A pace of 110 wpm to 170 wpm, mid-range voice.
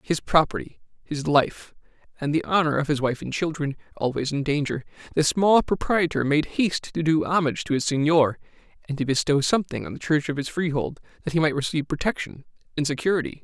No: average, 190 wpm; medium, 150 Hz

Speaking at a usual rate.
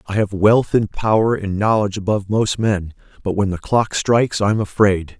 No: fast, 210 wpm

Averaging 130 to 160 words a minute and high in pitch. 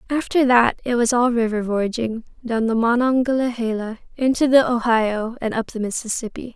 Yes: average, 155 wpm; high, 235 Hz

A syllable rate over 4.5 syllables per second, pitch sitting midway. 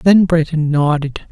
No: 3.9 syllables/s; medium, 160 Hz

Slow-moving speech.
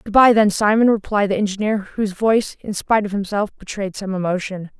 No: average, 200 wpm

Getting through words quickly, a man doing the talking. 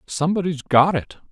No: slow, 135 wpm; male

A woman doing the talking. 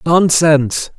No: male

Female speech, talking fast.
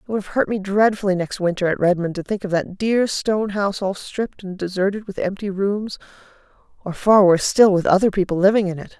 Yes: female; fast, 225 wpm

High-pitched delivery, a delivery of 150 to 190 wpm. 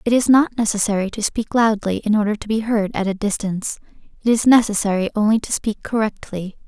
No: high, 215 Hz; average, 200 wpm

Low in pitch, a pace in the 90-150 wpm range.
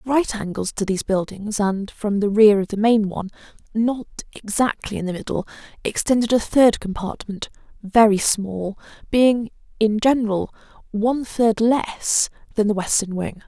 No: high, 215 Hz; average, 145 wpm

